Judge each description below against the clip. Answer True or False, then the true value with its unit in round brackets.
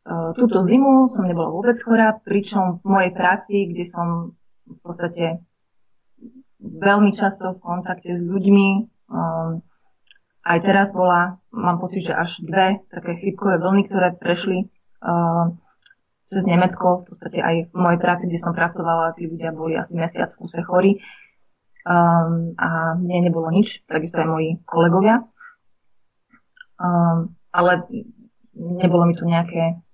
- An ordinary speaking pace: True (135 wpm)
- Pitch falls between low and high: True (180 Hz)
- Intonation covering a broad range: False (2.6 semitones)